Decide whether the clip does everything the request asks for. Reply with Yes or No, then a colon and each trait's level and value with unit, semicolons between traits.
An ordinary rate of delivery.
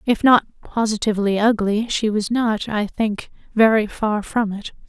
Yes: average, 160 wpm